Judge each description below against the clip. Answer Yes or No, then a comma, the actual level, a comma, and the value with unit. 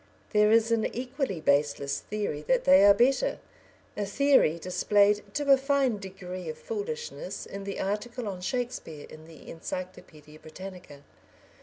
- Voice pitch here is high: Yes, high, 205 Hz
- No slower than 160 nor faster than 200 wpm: No, average, 145 wpm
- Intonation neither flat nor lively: No, wide, 6.0 semitones